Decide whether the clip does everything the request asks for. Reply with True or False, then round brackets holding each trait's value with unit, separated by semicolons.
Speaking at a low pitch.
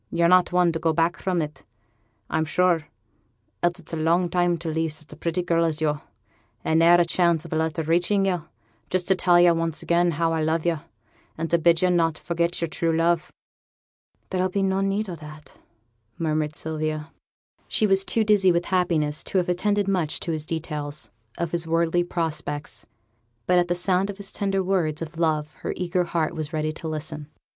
False (170 Hz)